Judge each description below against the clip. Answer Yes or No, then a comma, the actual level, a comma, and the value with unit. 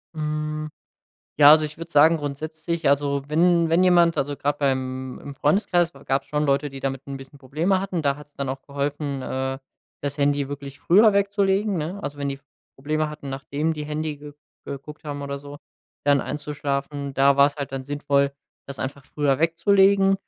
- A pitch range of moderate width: No, narrow, 2.2 semitones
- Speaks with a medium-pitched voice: Yes, medium, 145 Hz